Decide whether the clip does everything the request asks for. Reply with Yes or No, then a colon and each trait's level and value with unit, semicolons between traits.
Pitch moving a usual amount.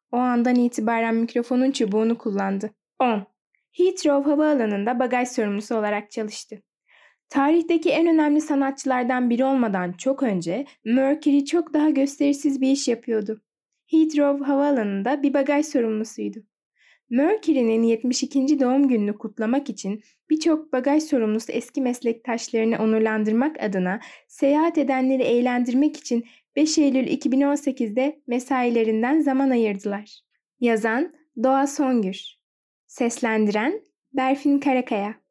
Yes: average, 4.1 semitones